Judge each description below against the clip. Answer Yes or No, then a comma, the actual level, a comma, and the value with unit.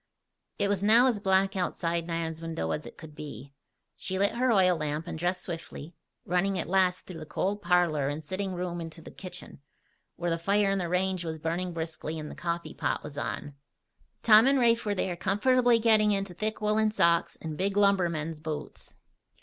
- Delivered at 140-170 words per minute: No, average, 195 wpm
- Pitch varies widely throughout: No, average, 3.6 semitones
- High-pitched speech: No, medium, 180 Hz